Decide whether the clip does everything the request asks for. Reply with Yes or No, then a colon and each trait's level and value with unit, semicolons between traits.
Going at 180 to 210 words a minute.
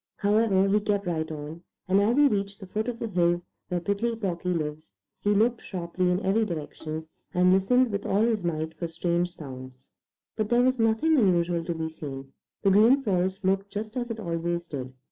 Yes: average, 200 wpm